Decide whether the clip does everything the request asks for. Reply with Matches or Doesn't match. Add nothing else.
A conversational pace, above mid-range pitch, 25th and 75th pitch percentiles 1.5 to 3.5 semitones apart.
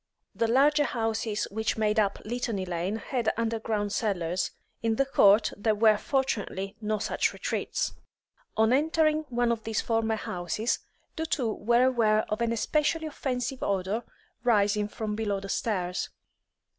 Matches